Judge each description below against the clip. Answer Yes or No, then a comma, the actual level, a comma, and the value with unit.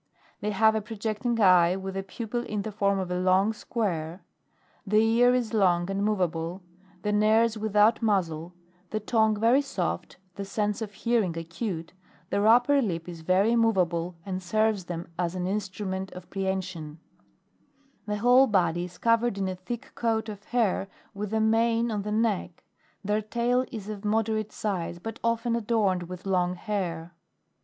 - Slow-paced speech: No, average, 165 wpm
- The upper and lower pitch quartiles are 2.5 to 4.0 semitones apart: Yes, average, 3.4 semitones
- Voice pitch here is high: Yes, high, 205 Hz